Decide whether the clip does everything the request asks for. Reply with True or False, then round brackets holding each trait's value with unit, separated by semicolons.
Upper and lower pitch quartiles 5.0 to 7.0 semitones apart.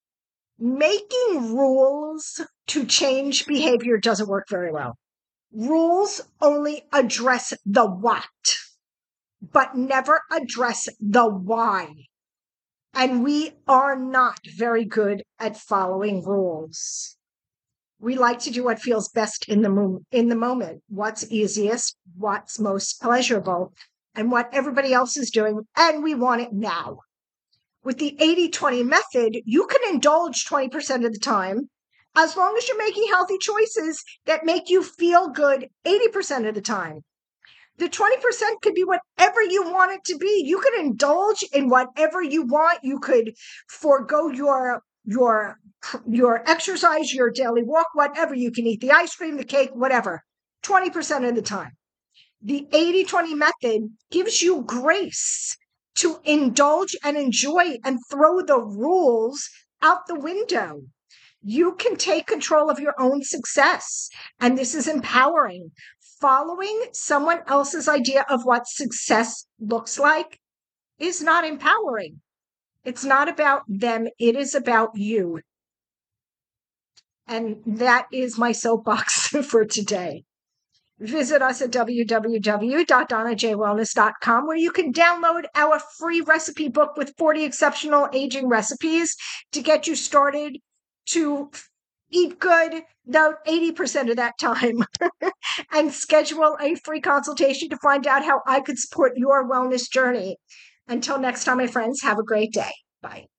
True (5.5 semitones)